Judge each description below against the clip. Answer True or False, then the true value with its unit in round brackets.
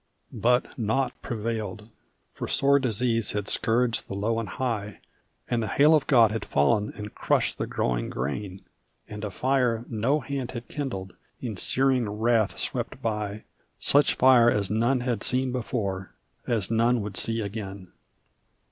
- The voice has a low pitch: True (115 Hz)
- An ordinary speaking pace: True (155 wpm)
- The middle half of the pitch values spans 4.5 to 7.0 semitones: False (3.2 semitones)